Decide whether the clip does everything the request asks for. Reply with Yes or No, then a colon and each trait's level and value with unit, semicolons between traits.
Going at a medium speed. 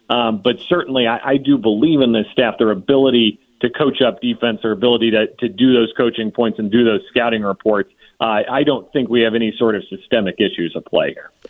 No: fast, 225 wpm